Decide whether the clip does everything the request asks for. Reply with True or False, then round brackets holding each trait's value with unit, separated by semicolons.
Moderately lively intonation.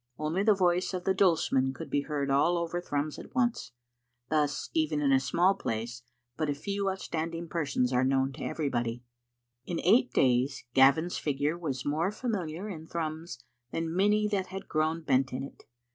True (4.5 semitones)